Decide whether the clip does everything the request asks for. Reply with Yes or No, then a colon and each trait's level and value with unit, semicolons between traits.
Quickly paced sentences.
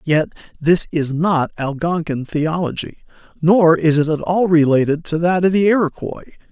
No: average, 155 wpm